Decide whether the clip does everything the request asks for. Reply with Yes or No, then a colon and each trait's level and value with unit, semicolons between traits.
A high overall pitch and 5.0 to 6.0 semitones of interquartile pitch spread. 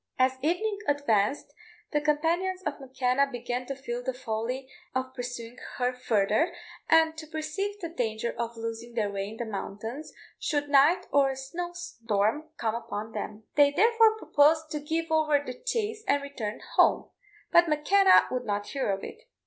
Yes: very high, 275 Hz; average, 5.3 semitones